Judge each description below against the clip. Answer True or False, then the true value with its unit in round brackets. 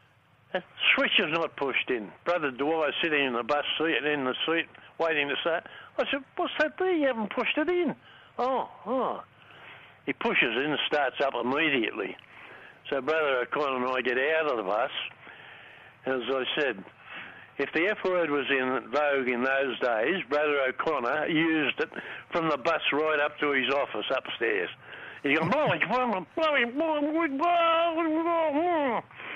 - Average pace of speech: True (160 wpm)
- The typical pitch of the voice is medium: True (160 Hz)